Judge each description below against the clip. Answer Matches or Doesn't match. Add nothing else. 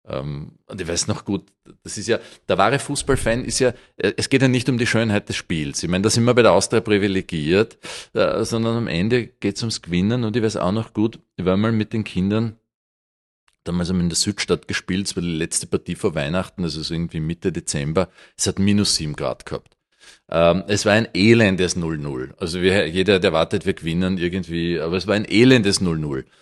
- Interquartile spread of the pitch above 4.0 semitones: Matches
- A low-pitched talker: Matches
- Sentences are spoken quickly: Matches